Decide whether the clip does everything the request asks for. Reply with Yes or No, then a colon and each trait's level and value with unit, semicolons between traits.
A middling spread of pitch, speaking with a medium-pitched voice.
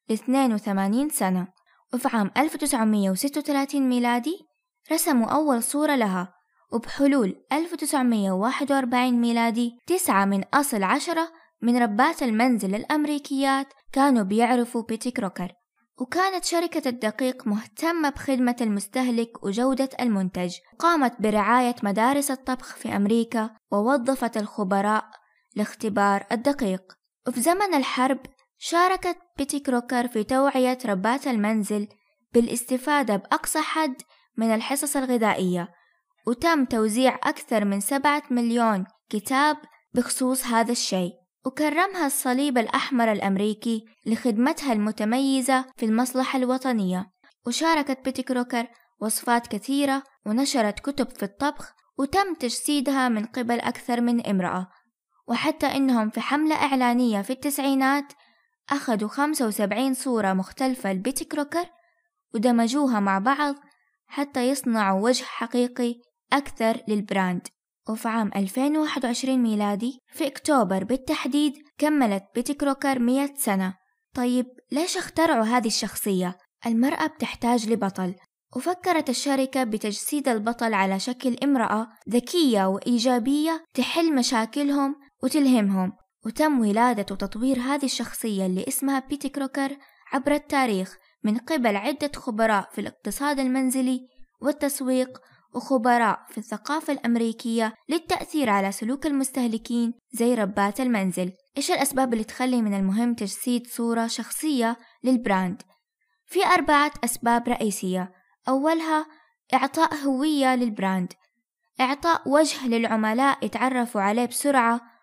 No: average, 4.0 semitones; very high, 250 Hz